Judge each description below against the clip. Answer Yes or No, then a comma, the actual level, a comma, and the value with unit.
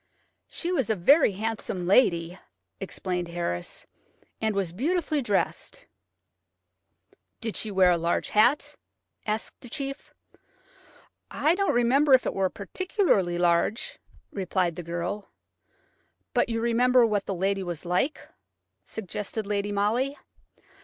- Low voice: No, high, 205 Hz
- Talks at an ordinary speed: No, slow, 125 wpm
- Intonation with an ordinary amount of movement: No, wide, 5.8 semitones